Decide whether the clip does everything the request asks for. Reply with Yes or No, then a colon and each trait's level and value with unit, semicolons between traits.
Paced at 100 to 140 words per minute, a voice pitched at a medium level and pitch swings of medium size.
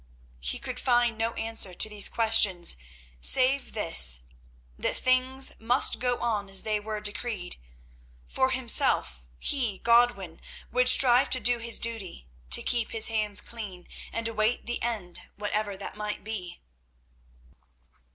No: slow, 135 wpm; high, 220 Hz; average, 3.9 semitones